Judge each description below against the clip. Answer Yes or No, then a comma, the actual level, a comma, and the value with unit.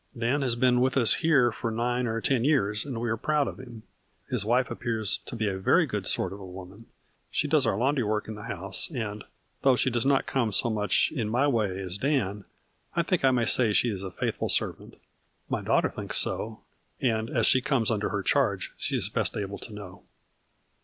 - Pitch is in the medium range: No, low, 115 Hz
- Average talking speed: No, fast, 220 wpm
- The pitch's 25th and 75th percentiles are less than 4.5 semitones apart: Yes, average, 3.7 semitones